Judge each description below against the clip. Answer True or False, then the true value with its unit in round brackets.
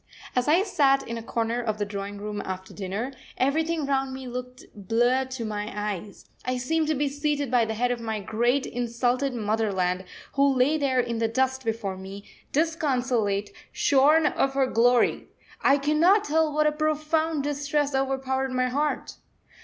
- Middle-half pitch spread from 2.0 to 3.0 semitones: False (4.3 semitones)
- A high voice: True (255 Hz)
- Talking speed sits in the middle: True (170 wpm)